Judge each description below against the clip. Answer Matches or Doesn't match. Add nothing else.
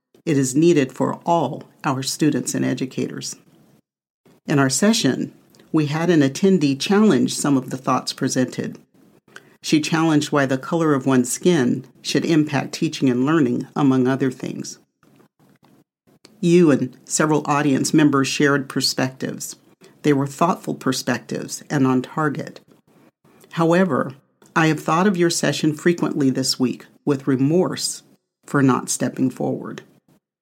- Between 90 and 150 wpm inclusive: Matches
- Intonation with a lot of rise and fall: Doesn't match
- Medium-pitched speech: Matches